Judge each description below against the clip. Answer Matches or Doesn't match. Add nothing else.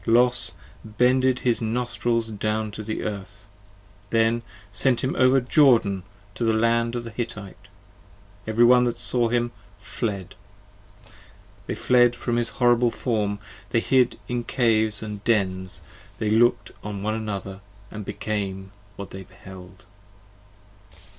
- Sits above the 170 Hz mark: Doesn't match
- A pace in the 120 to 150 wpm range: Matches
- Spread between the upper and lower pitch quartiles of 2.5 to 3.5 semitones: Matches